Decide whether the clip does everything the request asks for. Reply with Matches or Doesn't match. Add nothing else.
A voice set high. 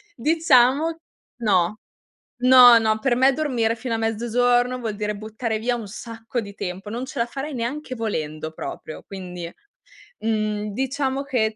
Matches